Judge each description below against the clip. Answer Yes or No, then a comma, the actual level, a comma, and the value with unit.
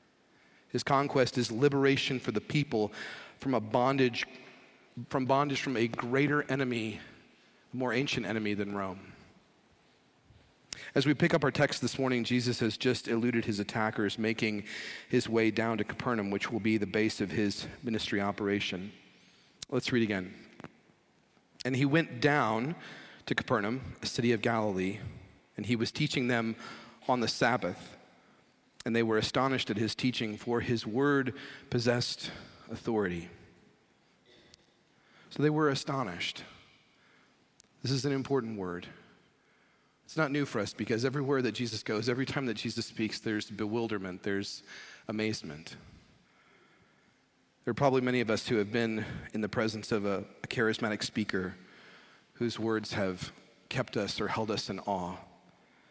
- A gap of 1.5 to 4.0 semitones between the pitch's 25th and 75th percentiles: Yes, average, 3.5 semitones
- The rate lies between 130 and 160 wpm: Yes, average, 150 wpm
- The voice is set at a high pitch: No, low, 115 Hz